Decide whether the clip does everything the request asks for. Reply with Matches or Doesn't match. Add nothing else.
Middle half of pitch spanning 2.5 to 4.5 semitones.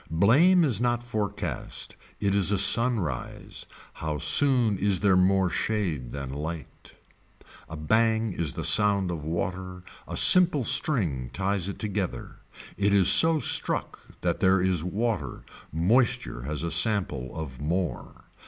Doesn't match